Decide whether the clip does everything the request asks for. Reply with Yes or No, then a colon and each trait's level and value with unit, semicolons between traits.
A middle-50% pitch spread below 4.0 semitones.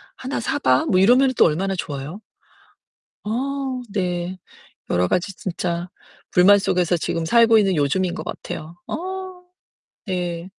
No: average, 5.2 semitones